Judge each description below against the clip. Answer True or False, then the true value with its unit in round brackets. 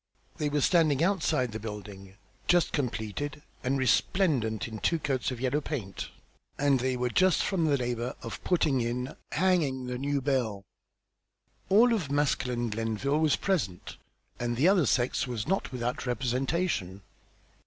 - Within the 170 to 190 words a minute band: False (150 wpm)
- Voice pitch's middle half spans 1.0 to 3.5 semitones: False (4.3 semitones)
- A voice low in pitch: True (130 Hz)